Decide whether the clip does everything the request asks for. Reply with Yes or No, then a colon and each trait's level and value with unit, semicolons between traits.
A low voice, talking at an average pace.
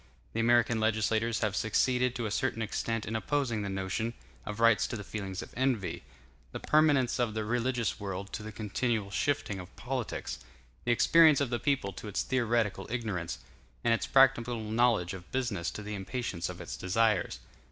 Yes: low, 115 Hz; average, 180 wpm